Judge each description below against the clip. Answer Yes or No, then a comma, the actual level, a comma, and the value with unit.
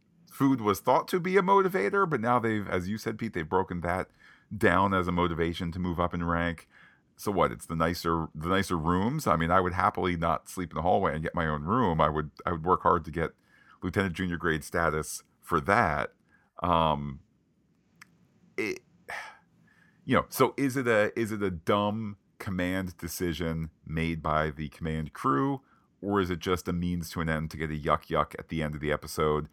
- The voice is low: Yes, very low, 90 Hz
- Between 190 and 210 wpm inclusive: Yes, fast, 205 wpm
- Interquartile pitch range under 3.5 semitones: No, average, 4.0 semitones